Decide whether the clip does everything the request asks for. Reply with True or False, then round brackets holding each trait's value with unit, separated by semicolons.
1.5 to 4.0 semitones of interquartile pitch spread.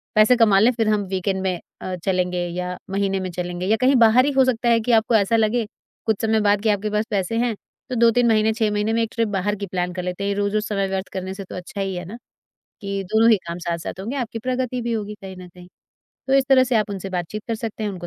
True (3.2 semitones)